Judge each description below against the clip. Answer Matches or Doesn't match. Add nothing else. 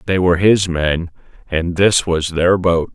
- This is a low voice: Matches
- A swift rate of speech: Doesn't match